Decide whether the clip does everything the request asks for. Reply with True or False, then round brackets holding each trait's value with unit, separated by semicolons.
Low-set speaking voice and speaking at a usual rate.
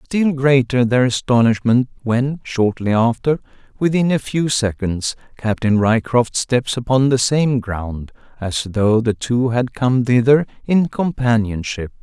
False (120 Hz; 130 wpm)